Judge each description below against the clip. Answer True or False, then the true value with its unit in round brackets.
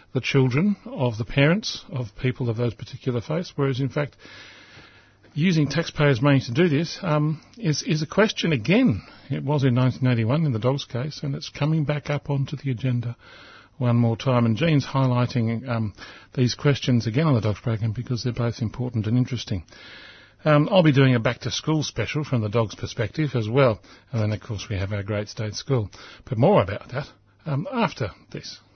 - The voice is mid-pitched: False (130 Hz)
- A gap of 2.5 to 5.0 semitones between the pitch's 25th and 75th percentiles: True (4.0 semitones)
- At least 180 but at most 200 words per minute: True (190 wpm)